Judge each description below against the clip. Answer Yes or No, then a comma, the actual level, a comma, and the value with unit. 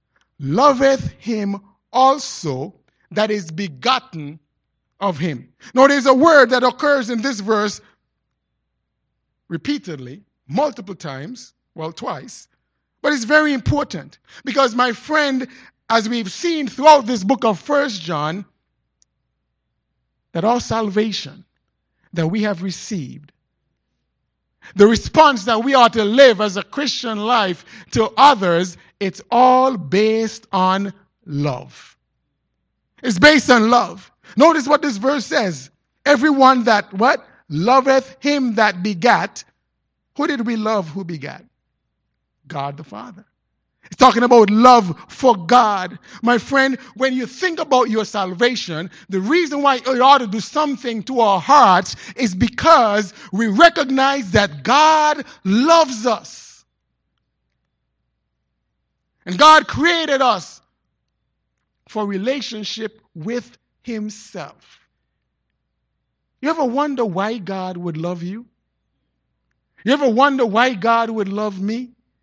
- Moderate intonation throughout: No, wide, 6.2 semitones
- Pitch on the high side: Yes, high, 225 Hz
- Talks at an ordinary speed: No, slow, 120 wpm